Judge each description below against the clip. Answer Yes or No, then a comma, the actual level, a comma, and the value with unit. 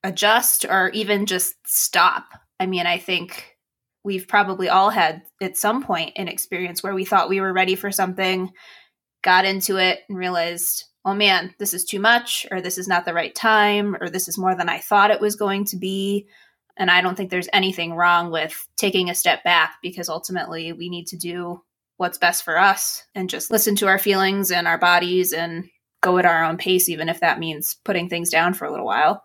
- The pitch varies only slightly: Yes, narrow, 2.1 semitones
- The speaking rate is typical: No, fast, 220 wpm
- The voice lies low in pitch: No, medium, 185 Hz